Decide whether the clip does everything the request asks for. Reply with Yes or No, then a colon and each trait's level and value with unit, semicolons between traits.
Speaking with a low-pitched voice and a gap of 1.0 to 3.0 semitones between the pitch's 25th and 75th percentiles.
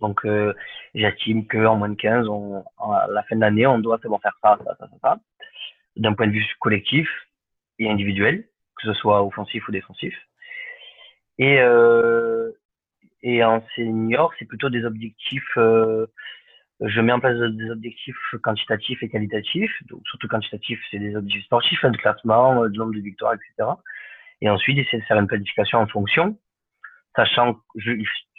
Yes: low, 115 Hz; narrow, 2.4 semitones